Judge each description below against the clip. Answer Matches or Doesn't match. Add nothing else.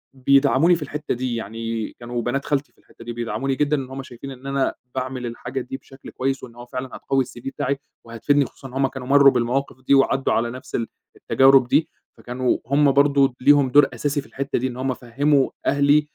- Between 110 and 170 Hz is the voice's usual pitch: Matches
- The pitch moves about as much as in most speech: Doesn't match